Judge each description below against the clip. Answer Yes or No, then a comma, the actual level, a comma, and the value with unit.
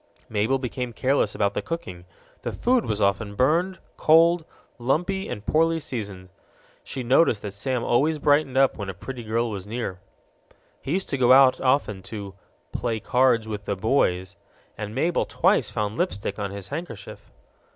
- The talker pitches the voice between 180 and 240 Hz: No, low, 120 Hz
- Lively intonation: Yes, wide, 5.9 semitones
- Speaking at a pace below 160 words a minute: No, average, 165 wpm